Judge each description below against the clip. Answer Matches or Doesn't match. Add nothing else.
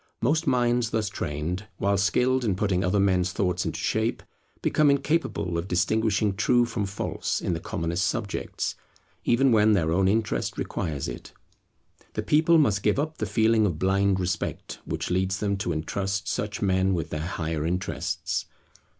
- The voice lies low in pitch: Matches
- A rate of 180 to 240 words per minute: Doesn't match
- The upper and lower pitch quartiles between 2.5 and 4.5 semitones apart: Matches